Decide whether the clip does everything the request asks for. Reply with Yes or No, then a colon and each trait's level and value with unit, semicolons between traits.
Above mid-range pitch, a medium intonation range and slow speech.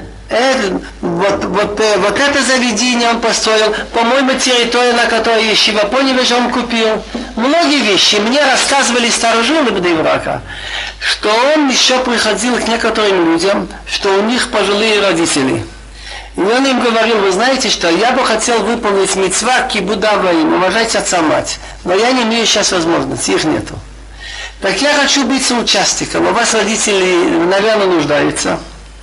No: high, 225 Hz; average, 3.3 semitones; average, 145 wpm